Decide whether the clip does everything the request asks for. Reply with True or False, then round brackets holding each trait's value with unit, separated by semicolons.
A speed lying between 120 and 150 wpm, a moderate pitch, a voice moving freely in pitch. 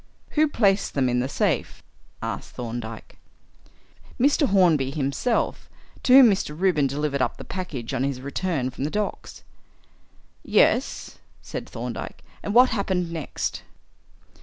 True (135 wpm; 155 Hz; 7.0 semitones)